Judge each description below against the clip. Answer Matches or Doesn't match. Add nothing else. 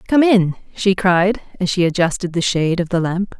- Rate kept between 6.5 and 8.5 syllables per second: Doesn't match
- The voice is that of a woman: Matches